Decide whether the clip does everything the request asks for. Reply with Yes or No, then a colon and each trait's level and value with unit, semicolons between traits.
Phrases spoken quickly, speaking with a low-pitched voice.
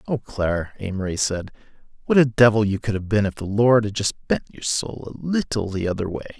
Yes: fast, 225 wpm; low, 105 Hz